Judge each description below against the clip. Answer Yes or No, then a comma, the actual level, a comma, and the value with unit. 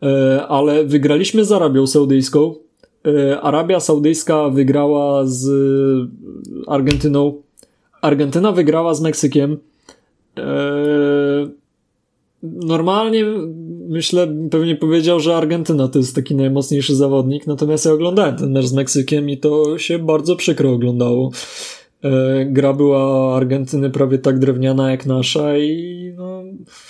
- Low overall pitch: No, medium, 145 Hz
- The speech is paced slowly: Yes, slow, 105 wpm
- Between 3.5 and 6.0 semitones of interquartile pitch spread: No, average, 2.9 semitones